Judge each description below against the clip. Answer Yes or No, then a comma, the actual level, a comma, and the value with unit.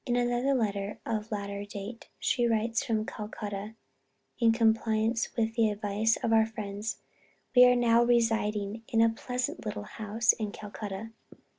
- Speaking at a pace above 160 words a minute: No, average, 155 wpm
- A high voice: Yes, high, 225 Hz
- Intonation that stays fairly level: Yes, narrow, 1.8 semitones